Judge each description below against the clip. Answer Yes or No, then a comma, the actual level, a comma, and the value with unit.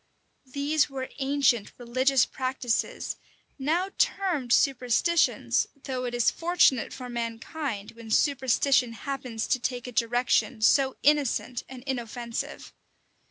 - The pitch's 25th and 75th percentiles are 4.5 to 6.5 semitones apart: No, average, 2.8 semitones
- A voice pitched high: Yes, very high, 255 Hz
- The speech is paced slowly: Yes, slow, 115 wpm